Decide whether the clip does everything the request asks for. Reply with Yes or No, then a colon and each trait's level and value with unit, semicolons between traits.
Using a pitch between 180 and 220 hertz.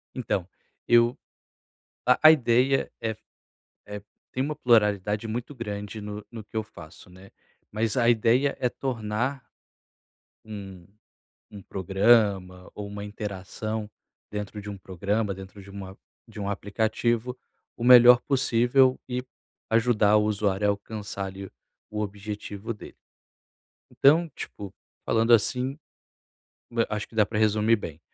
No: low, 105 Hz